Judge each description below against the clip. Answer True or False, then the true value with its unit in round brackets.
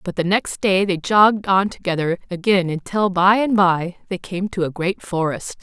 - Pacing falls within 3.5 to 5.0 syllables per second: True (4.7 syllables/s)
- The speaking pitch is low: False (185 Hz)